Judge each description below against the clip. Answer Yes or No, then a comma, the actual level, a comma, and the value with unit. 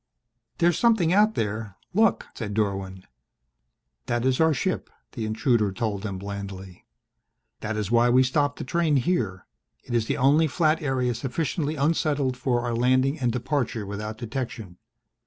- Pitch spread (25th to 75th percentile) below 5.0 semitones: No, average, 5.3 semitones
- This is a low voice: Yes, low, 125 Hz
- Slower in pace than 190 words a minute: Yes, average, 155 wpm